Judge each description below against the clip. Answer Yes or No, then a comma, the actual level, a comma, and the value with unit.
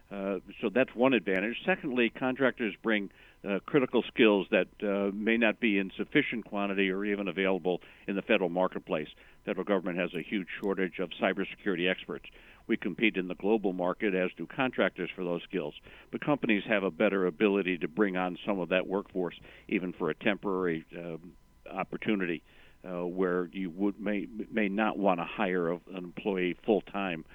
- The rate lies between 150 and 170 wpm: No, average, 180 wpm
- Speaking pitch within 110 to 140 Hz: No, very low, 95 Hz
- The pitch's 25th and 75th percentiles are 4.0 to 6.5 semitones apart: No, narrow, 2.5 semitones